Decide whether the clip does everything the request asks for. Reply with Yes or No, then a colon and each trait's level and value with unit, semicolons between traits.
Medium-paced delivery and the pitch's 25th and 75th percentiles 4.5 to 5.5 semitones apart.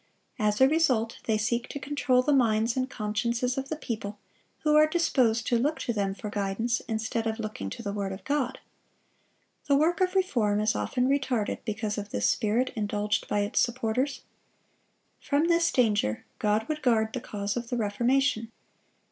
No: average, 180 wpm; average, 4.1 semitones